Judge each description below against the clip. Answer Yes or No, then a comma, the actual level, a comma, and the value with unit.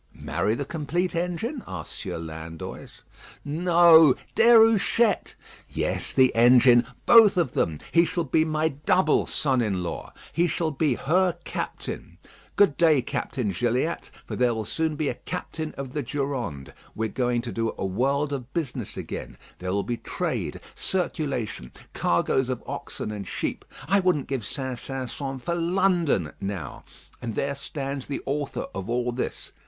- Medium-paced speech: Yes, average, 160 wpm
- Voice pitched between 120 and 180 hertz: Yes, low, 135 Hz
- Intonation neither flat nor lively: No, wide, 6.0 semitones